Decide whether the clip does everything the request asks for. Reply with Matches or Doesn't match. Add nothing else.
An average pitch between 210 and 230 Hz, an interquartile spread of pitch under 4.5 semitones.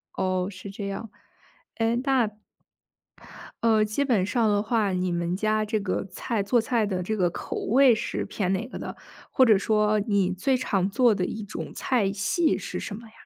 Matches